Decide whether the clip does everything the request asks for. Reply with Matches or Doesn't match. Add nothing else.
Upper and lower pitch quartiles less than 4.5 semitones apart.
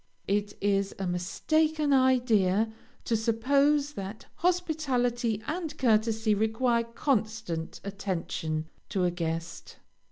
Doesn't match